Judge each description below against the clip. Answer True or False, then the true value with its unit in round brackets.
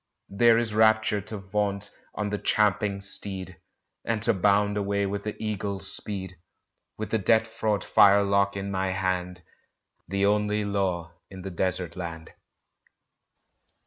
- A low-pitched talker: True (100 Hz)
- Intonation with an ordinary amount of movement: False (1.8 semitones)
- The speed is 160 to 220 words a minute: False (140 wpm)